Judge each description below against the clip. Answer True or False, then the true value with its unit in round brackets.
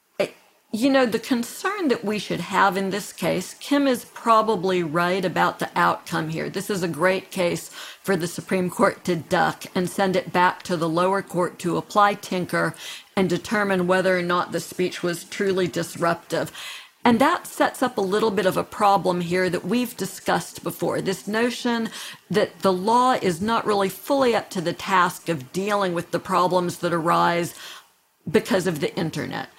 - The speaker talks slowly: False (185 wpm)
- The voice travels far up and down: False (2.9 semitones)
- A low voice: False (190 Hz)